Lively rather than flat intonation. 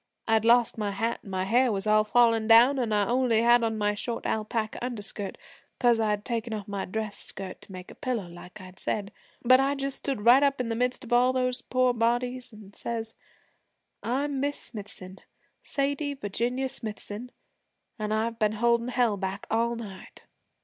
No: average, 3.0 semitones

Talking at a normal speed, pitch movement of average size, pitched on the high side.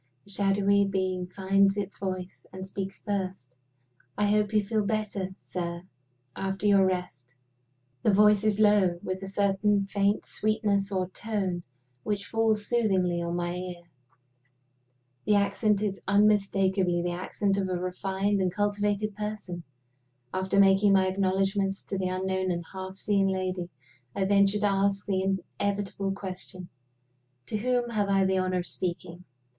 No: average, 150 wpm; narrow, 1.6 semitones; high, 195 Hz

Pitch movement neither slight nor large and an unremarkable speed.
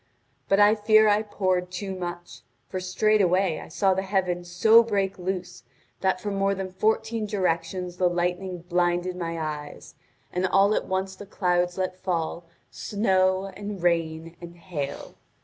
No: narrow, 1.9 semitones; average, 155 wpm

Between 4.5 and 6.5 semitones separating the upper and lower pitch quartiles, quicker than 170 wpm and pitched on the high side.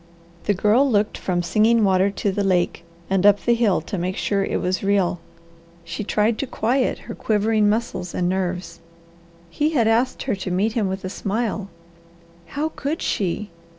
No: average, 3.3 semitones; average, 180 wpm; high, 205 Hz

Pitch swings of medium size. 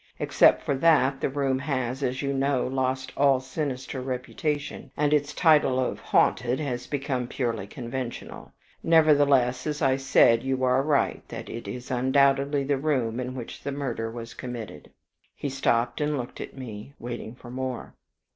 No: narrow, 2.2 semitones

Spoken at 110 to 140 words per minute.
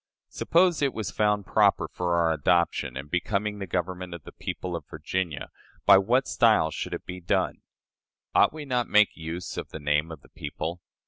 No: average, 195 wpm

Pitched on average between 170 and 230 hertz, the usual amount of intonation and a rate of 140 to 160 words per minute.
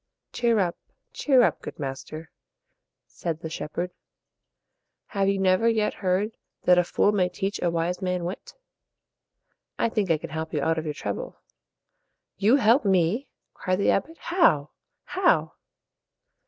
Yes: medium, 185 Hz; average, 4.3 semitones; average, 150 wpm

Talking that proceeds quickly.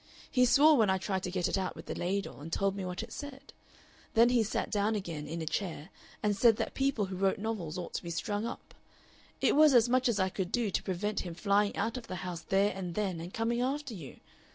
Yes: fast, 250 wpm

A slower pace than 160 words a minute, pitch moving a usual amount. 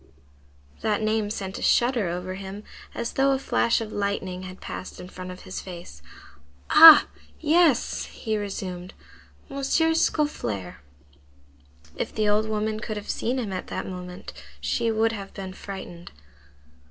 Yes: average, 150 wpm; average, 3.7 semitones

